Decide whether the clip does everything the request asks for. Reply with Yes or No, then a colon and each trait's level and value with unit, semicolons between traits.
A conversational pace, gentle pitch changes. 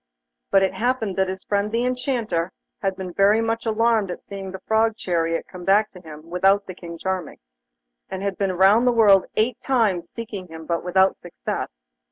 No: average, 190 wpm; average, 3.5 semitones